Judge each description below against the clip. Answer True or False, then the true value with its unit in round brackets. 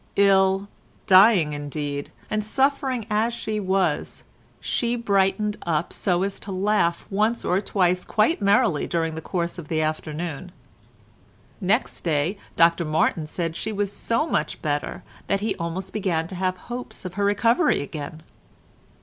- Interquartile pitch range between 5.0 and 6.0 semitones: False (4.3 semitones)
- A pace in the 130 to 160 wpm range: True (150 wpm)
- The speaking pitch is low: False (190 Hz)